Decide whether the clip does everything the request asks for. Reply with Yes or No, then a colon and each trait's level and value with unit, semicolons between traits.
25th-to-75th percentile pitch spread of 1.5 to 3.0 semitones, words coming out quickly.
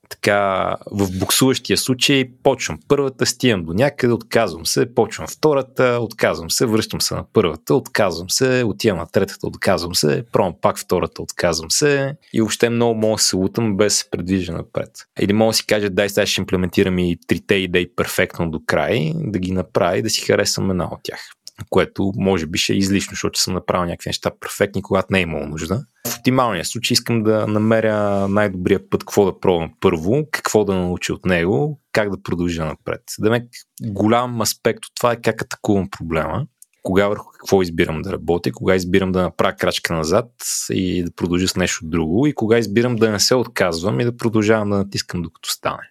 No: average, 4.0 semitones; fast, 190 wpm